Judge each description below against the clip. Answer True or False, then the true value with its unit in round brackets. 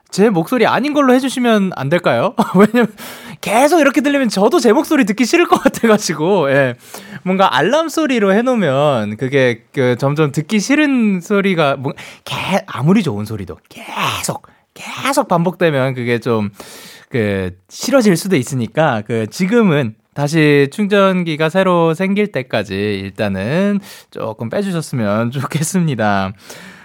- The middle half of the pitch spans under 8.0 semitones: False (9.0 semitones)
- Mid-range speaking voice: True (180 Hz)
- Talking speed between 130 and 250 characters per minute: False (295 characters per minute)